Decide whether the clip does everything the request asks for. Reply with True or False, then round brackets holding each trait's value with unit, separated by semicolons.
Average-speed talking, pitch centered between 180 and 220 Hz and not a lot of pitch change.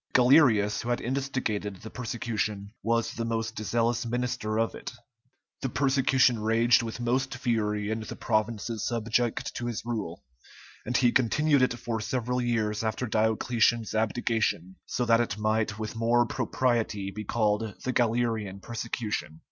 False (150 wpm; 115 Hz; 2.1 semitones)